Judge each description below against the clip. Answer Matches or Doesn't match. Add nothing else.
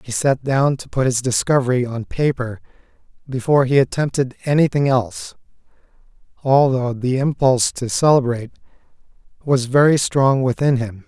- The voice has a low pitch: Matches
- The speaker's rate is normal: Doesn't match